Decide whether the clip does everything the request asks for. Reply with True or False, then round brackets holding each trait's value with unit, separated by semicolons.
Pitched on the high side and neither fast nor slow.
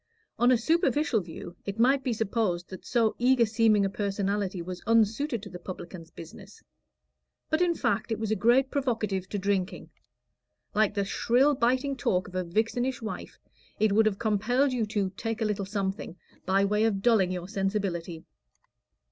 True (215 Hz; 175 wpm)